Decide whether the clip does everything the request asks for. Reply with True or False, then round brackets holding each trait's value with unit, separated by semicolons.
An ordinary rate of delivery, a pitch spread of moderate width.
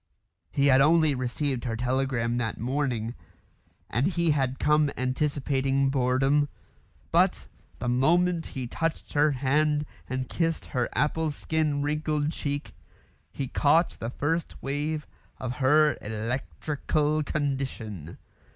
False (120 wpm; 3.0 semitones)